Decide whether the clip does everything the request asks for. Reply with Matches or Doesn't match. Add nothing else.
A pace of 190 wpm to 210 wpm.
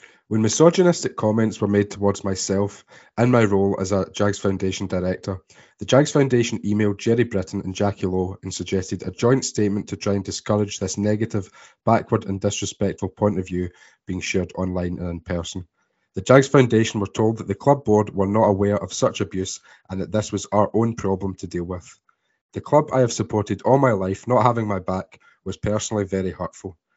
Matches